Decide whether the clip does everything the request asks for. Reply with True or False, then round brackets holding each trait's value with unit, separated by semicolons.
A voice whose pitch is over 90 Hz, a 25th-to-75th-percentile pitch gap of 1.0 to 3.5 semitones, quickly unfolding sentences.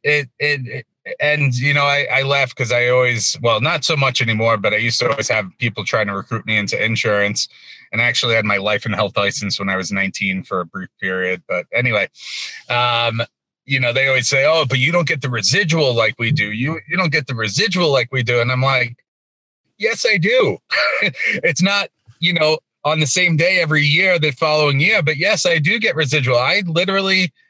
False (135 Hz; 5.5 semitones; 220 wpm)